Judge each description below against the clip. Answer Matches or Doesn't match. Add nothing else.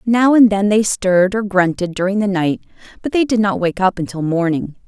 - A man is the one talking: Doesn't match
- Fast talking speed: Matches